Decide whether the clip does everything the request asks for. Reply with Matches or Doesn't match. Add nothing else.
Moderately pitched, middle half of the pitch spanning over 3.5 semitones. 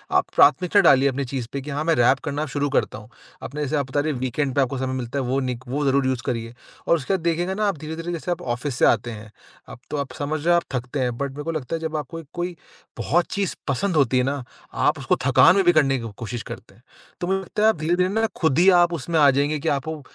Matches